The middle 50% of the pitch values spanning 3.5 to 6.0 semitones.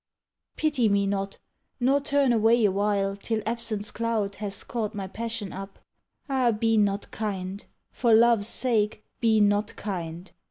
No: narrow, 2.6 semitones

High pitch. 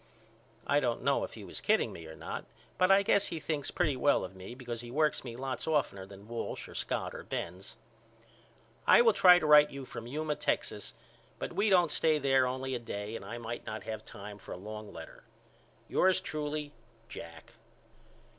No: low, 130 Hz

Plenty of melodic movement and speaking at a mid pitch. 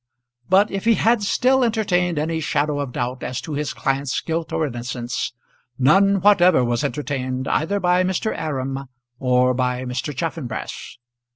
Yes: wide, 6.3 semitones; medium, 150 Hz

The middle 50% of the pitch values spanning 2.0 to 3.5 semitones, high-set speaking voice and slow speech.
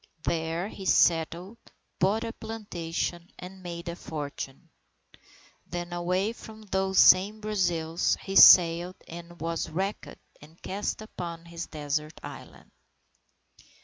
No: narrow, 2.6 semitones; medium, 175 Hz; slow, 115 wpm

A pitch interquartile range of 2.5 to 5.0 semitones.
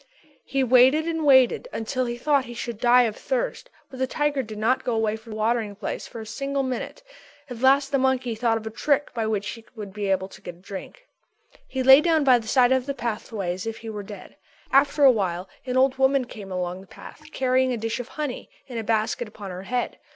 Yes: average, 3.5 semitones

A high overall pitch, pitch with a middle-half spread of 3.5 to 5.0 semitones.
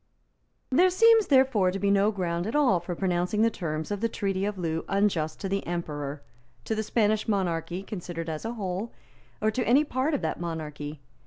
Yes: high, 195 Hz; average, 4.6 semitones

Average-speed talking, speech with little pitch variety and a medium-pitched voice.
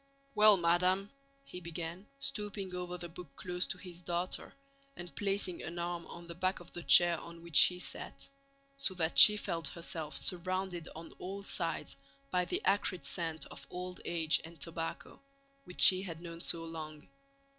Yes: average, 170 wpm; narrow, 1.7 semitones; medium, 175 Hz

